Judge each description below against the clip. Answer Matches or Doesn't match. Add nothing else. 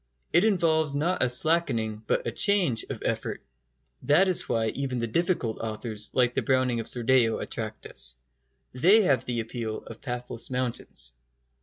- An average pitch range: Doesn't match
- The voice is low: Matches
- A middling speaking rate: Matches